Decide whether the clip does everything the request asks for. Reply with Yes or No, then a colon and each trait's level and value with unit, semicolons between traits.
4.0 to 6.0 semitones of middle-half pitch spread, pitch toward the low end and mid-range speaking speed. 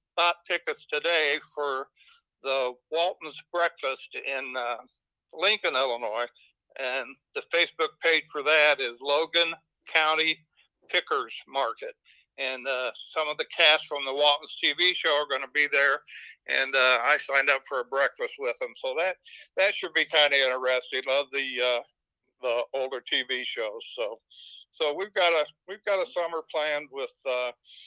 No: wide, 5.6 semitones; medium, 155 Hz; average, 160 wpm